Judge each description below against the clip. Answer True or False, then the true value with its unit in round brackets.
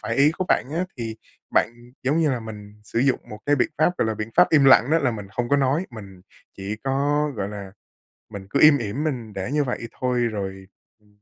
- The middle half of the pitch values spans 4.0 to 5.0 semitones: False (5.4 semitones)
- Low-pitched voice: True (120 Hz)